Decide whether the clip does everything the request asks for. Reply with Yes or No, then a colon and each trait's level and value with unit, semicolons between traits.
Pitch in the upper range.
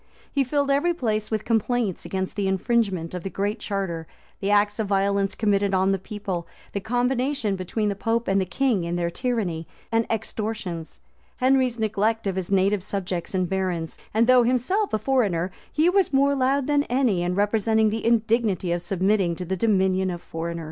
Yes: high, 205 Hz